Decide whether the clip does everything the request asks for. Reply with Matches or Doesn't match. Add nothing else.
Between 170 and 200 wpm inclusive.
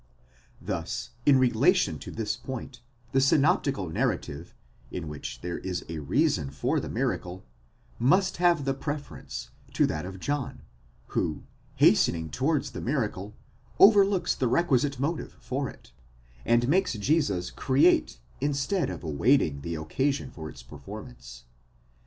Doesn't match